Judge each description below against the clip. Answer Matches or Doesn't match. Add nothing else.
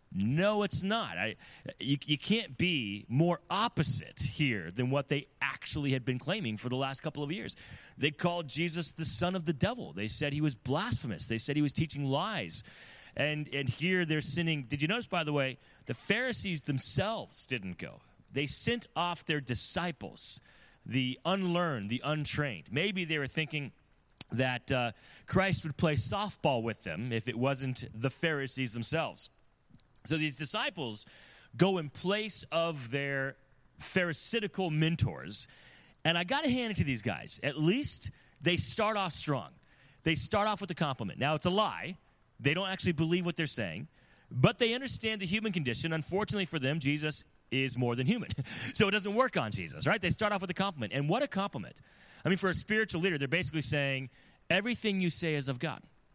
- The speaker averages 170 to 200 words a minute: Matches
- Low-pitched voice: Doesn't match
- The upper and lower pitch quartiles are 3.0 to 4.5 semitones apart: Doesn't match